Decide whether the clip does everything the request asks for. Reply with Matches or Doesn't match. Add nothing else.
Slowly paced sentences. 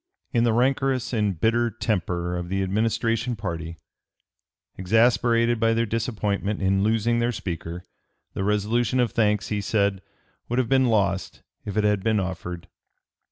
Doesn't match